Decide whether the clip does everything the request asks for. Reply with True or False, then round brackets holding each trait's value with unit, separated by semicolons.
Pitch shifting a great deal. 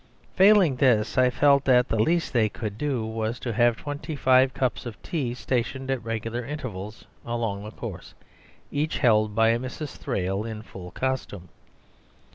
False (3.5 semitones)